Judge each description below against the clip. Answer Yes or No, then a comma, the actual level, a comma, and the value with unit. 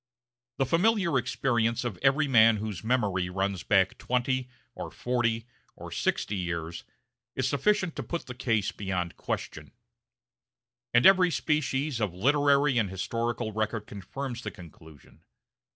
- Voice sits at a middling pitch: No, low, 120 Hz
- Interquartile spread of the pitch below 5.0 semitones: No, average, 5.3 semitones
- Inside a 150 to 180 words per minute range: No, slow, 135 wpm